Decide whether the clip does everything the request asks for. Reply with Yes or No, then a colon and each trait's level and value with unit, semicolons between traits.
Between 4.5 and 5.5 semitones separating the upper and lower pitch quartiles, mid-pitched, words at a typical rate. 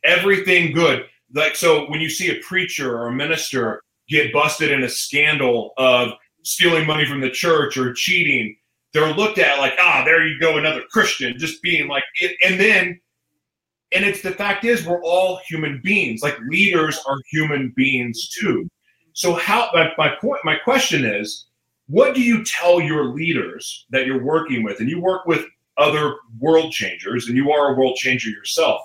Yes: average, 5.1 semitones; medium, 155 Hz; average, 180 wpm